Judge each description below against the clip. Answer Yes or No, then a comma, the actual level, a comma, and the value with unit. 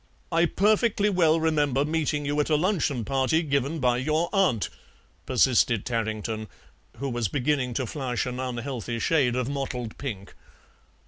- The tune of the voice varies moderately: Yes, average, 4.4 semitones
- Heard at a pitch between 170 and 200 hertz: No, low, 135 Hz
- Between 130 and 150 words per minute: Yes, average, 145 wpm